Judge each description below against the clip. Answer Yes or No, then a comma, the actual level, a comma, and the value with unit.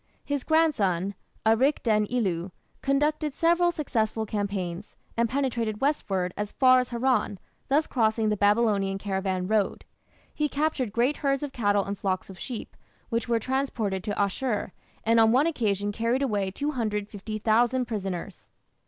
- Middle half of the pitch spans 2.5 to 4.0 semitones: No, average, 4.6 semitones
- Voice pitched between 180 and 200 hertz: No, high, 225 Hz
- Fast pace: No, average, 145 wpm